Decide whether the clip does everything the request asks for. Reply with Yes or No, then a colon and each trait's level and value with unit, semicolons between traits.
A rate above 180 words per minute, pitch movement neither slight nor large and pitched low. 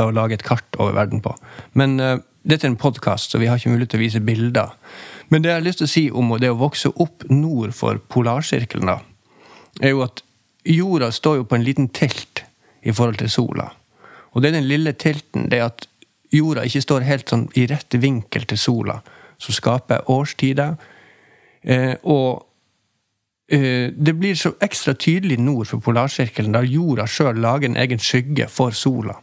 Yes: fast, 195 wpm; average, 3.7 semitones; low, 130 Hz